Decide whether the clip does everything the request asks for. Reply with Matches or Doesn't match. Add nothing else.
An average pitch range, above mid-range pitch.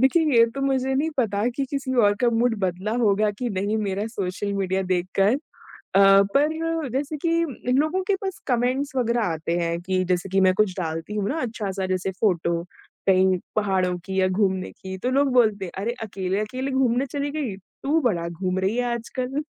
Doesn't match